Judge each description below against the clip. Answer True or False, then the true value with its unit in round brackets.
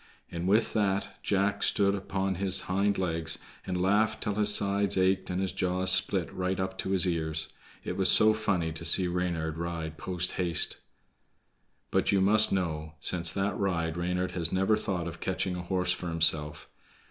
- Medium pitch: False (90 Hz)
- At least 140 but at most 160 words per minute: False (180 wpm)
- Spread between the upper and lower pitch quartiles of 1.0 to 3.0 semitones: True (2.5 semitones)